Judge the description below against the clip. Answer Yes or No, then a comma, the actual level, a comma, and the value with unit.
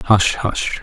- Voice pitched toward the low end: Yes, low, 100 Hz